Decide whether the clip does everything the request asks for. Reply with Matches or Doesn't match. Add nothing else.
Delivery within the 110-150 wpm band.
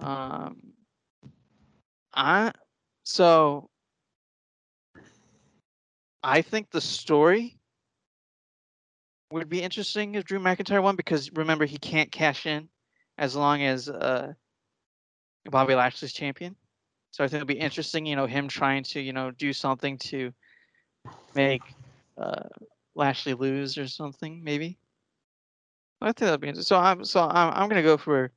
Matches